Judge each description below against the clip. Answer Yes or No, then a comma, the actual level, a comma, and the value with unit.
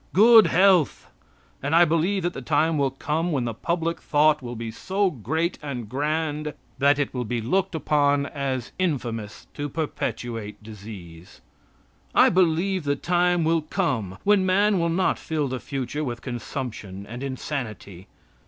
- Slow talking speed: No, average, 155 wpm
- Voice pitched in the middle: Yes, medium, 145 Hz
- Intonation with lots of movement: Yes, wide, 5.7 semitones